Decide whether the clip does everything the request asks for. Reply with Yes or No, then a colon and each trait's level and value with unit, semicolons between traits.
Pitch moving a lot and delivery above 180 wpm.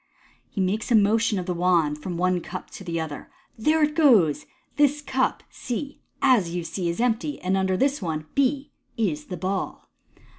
Yes: wide, 6.8 semitones; average, 195 wpm